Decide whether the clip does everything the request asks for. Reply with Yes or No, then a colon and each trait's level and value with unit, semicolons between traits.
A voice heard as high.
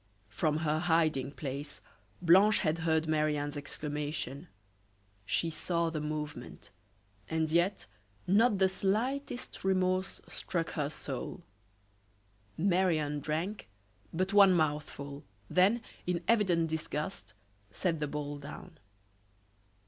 No: medium, 160 Hz